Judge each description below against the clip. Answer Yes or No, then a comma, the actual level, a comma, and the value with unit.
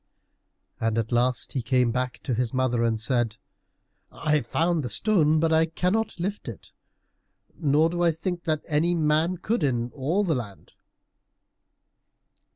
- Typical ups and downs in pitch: No, wide, 5.7 semitones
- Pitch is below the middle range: No, medium, 150 Hz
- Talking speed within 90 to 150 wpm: No, average, 160 wpm